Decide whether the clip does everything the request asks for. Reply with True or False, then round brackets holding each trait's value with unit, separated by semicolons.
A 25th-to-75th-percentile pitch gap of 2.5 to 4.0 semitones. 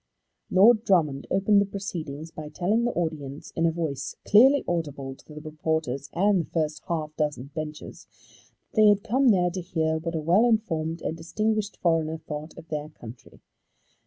False (4.4 semitones)